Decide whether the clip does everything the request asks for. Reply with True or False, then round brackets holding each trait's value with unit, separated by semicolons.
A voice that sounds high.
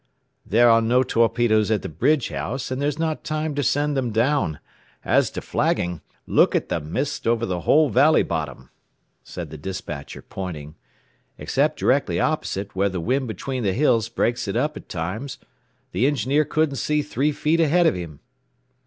False (120 Hz)